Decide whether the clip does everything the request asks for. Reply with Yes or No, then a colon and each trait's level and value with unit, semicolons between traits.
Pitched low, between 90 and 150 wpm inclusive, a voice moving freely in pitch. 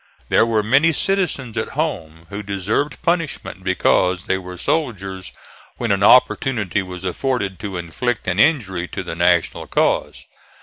Yes: low, 100 Hz; average, 145 wpm; wide, 6.0 semitones